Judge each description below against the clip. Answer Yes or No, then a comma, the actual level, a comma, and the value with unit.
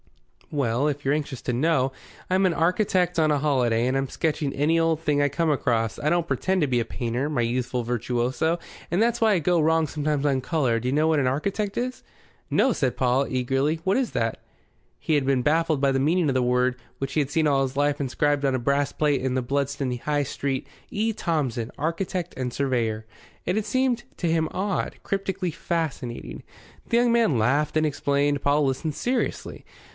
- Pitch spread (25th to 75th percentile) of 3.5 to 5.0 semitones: Yes, average, 4.1 semitones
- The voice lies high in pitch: No, medium, 145 Hz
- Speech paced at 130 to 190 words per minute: No, fast, 205 wpm